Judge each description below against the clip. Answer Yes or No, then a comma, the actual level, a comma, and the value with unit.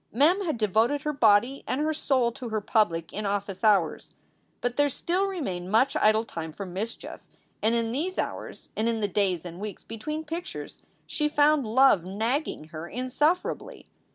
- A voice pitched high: Yes, high, 230 Hz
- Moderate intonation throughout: No, wide, 6.3 semitones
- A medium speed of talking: Yes, average, 175 wpm